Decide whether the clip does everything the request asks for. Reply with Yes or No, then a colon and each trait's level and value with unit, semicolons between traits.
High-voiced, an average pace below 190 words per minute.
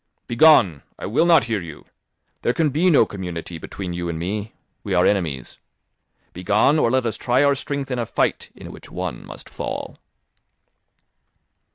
No: low, 110 Hz; average, 170 wpm